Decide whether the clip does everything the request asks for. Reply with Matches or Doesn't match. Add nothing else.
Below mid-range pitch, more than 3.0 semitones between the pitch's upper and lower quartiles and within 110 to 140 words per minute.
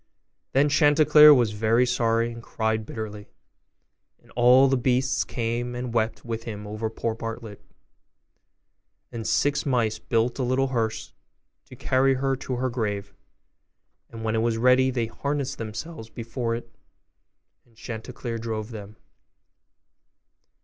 Doesn't match